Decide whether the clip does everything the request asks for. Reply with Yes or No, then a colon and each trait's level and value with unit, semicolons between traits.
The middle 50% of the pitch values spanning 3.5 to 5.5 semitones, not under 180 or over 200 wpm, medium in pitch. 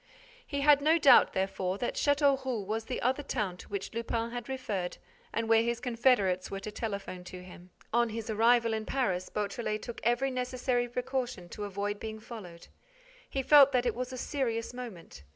No: average, 3.8 semitones; average, 185 wpm; high, 230 Hz